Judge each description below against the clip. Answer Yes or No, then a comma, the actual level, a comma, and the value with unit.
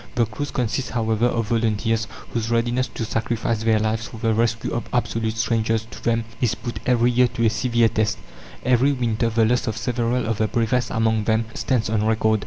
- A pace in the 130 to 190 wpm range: No, average, 200 wpm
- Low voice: Yes, low, 115 Hz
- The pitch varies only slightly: Yes, narrow, 1.3 semitones